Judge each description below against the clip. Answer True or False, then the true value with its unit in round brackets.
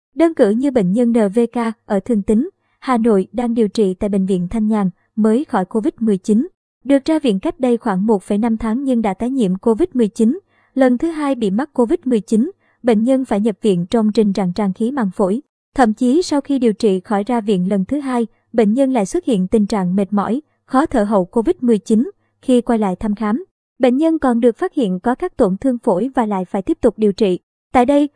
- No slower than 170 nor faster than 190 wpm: False (220 wpm)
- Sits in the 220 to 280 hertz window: True (230 Hz)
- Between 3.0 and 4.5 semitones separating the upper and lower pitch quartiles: True (3.6 semitones)